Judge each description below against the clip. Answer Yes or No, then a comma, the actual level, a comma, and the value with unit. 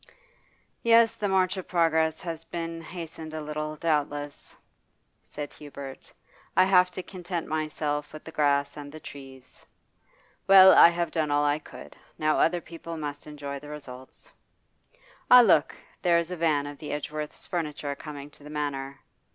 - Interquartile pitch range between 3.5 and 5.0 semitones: No, average, 2.7 semitones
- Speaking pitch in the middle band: Yes, medium, 155 Hz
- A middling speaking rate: Yes, average, 160 wpm